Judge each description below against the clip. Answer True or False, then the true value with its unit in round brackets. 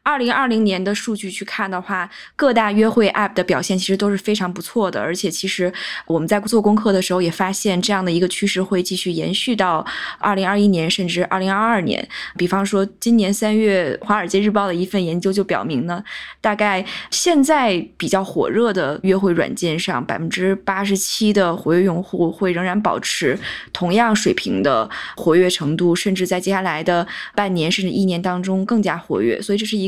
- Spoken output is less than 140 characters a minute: False (315 characters per minute)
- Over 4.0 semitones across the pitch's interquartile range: False (2.5 semitones)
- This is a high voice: True (195 Hz)